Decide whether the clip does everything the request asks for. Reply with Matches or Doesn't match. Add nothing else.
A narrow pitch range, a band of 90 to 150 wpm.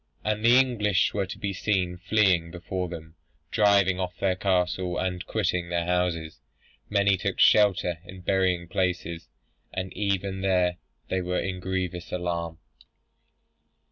Matches